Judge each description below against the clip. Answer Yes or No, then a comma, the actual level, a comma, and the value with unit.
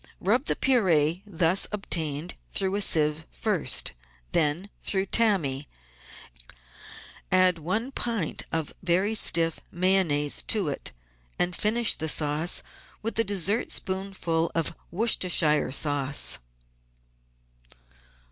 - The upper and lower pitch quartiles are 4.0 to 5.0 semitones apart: Yes, average, 4.5 semitones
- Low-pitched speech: No, medium, 175 Hz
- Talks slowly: Yes, slow, 100 wpm